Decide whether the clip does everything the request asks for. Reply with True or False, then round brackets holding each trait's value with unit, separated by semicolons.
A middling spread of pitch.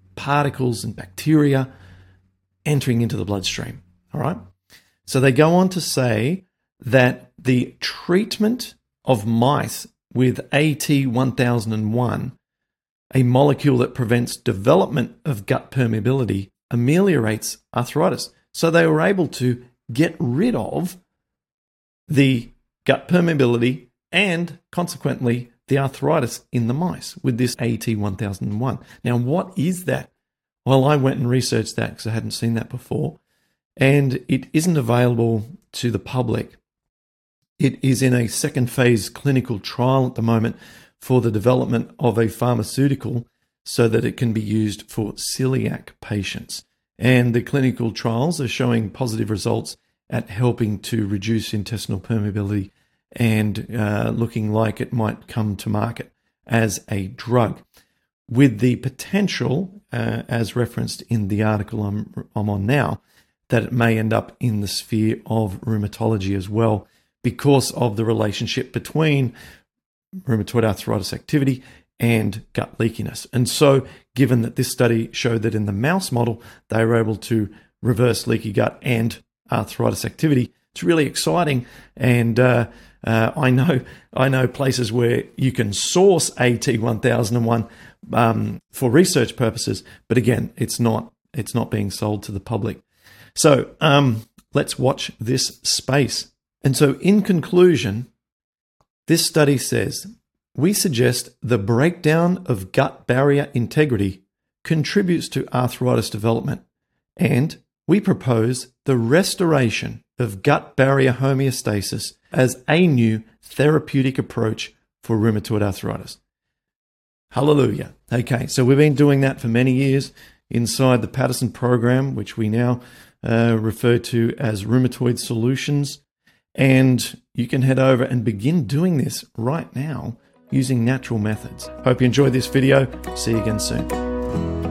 True (3.4 semitones)